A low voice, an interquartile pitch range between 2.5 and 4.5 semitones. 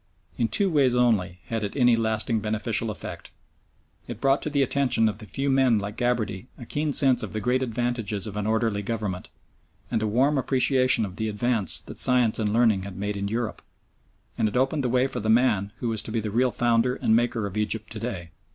Yes: low, 115 Hz; average, 2.9 semitones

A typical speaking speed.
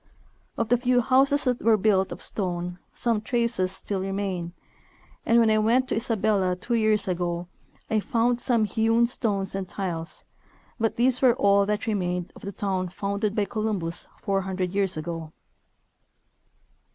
Yes: average, 160 wpm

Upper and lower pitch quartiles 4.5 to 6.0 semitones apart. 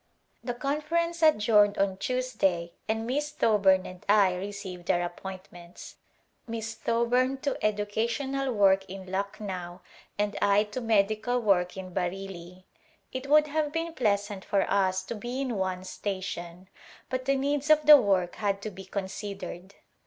Yes: average, 5.1 semitones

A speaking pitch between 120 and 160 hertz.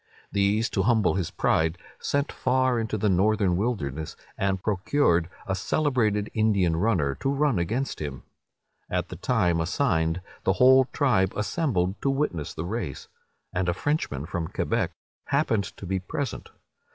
No: low, 100 Hz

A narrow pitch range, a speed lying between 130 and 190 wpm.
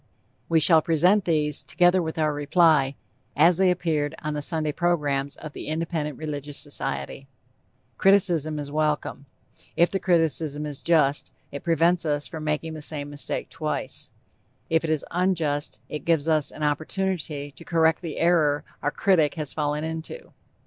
Yes: narrow, 2.3 semitones; average, 160 wpm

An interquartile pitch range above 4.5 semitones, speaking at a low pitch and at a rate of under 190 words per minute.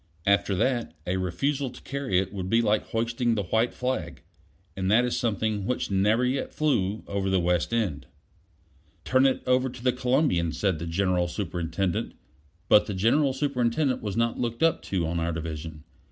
Yes: wide, 5.6 semitones; low, 105 Hz; average, 180 wpm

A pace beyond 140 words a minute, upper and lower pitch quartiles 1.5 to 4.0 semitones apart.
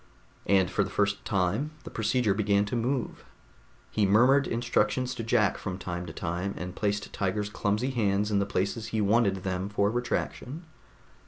Yes: average, 170 wpm; average, 3.1 semitones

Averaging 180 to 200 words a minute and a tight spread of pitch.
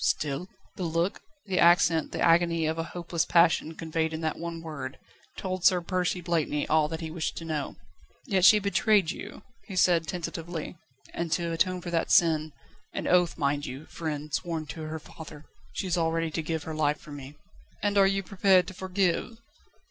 Yes: average, 190 wpm; narrow, 2.3 semitones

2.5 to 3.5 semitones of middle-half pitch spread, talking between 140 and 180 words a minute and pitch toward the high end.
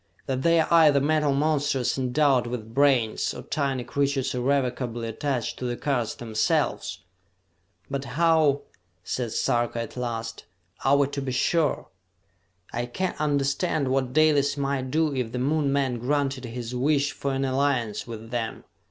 No: average, 2.8 semitones; average, 150 wpm; low, 135 Hz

